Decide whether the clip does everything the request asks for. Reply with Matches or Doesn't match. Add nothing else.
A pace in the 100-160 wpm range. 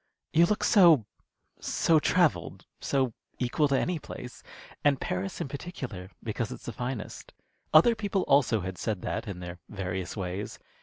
Matches